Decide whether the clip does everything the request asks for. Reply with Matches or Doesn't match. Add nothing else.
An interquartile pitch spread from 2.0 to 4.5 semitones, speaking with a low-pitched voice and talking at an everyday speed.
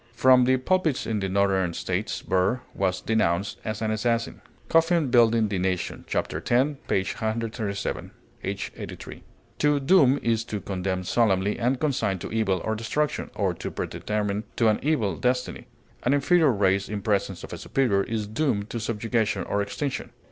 Matches